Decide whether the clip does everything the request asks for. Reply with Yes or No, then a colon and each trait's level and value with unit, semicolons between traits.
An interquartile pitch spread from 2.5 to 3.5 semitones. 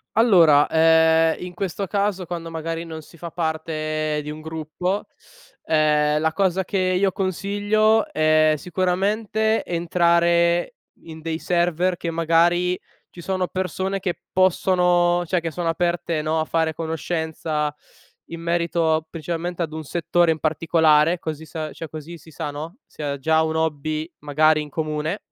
No: narrow, 2.1 semitones